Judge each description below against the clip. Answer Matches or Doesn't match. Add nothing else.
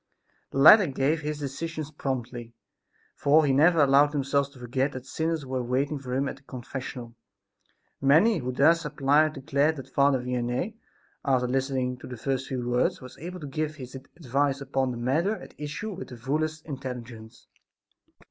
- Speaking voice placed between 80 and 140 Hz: Matches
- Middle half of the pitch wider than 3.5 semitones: Doesn't match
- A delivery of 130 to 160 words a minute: Doesn't match